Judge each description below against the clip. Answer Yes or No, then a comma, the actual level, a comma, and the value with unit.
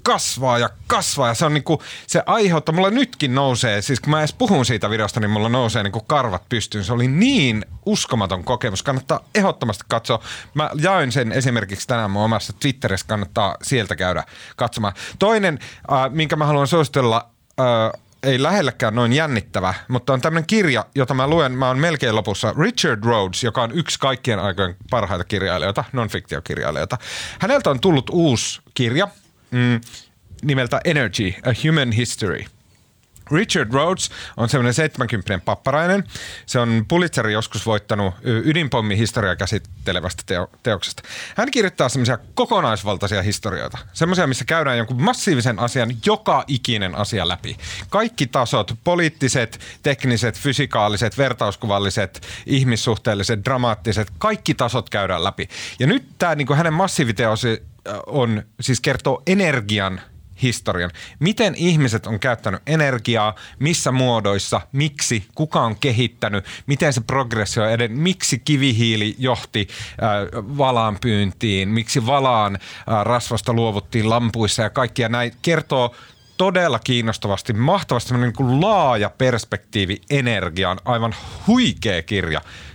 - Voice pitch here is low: Yes, low, 120 Hz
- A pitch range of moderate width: Yes, average, 5.0 semitones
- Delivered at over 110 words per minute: Yes, average, 130 wpm